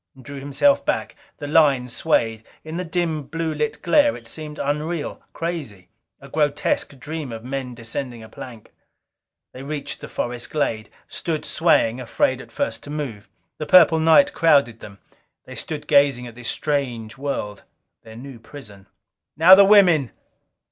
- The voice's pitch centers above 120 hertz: Yes, medium, 140 Hz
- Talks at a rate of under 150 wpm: No, average, 155 wpm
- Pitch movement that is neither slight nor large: Yes, average, 4.7 semitones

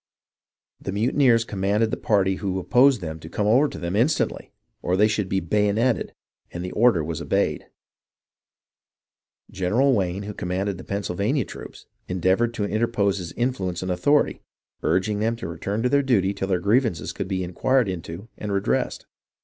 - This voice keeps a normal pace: Yes, average, 170 wpm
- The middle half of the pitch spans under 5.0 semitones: Yes, average, 3.9 semitones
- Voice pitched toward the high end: No, low, 100 Hz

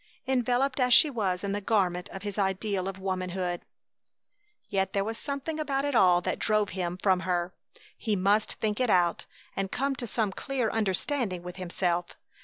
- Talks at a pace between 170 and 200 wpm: Yes, average, 180 wpm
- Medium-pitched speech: No, high, 200 Hz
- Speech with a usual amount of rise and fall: Yes, average, 4.6 semitones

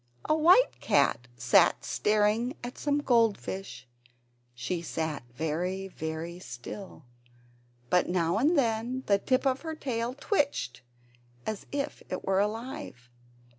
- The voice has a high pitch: Yes, high, 210 Hz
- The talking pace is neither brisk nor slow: No, slow, 125 wpm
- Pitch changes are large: Yes, wide, 7.8 semitones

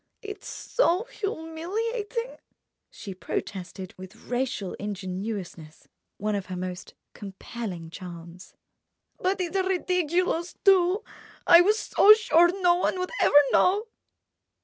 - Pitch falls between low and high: No, very high, 325 Hz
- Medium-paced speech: No, slow, 105 wpm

